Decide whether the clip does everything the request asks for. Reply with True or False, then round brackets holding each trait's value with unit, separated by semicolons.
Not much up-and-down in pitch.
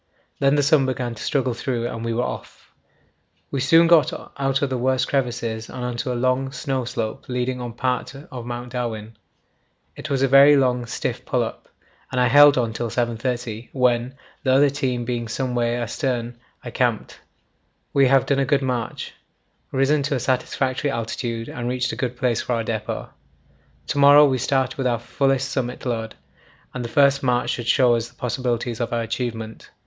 True (2.2 semitones)